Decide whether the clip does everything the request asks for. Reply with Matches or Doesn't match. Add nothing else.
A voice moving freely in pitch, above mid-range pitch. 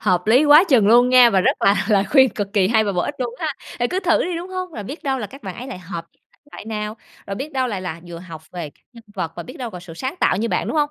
Matches